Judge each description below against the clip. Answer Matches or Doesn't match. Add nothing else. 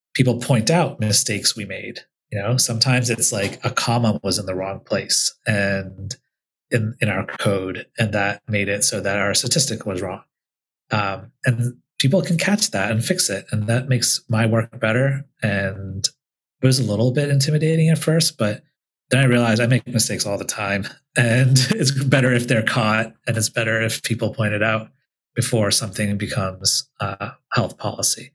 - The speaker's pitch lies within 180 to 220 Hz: Doesn't match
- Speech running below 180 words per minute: Doesn't match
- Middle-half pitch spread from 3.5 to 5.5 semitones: Matches